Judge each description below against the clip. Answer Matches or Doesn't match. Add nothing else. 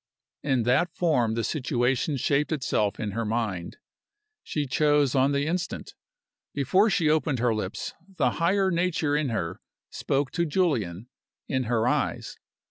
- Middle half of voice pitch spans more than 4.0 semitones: Matches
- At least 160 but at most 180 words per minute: Doesn't match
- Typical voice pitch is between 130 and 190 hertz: Matches